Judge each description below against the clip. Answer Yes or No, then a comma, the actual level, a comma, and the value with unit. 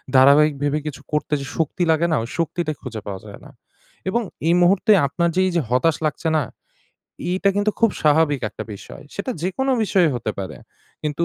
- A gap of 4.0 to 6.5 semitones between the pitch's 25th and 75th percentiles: Yes, average, 4.3 semitones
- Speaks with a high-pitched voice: No, medium, 155 Hz